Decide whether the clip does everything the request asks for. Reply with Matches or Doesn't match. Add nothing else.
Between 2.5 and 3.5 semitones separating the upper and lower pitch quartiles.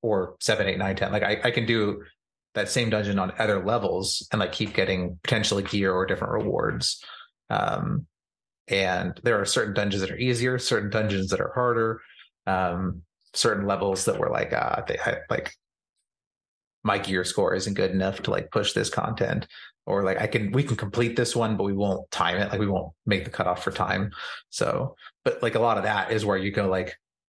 Matches